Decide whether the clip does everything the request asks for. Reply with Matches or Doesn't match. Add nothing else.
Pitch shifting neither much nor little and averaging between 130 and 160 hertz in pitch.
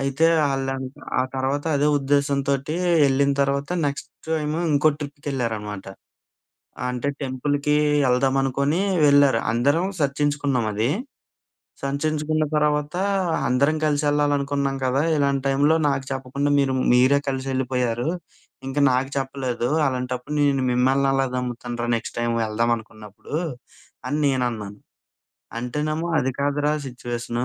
Doesn't match